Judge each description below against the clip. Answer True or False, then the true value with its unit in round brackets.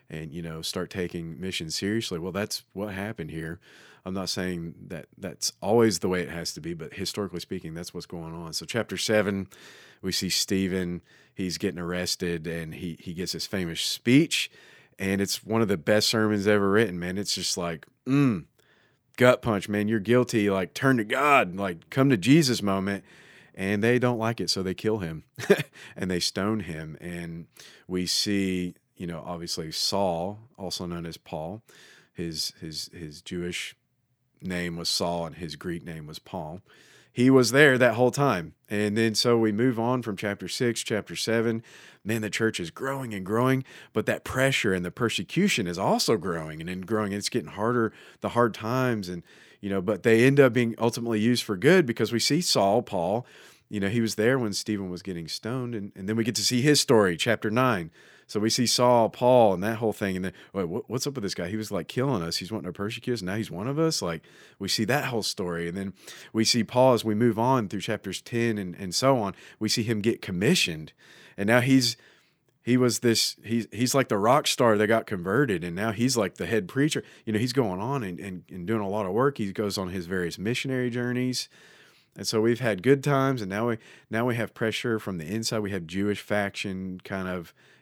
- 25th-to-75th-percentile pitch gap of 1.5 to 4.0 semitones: False (4.7 semitones)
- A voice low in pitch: True (105 Hz)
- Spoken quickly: True (215 wpm)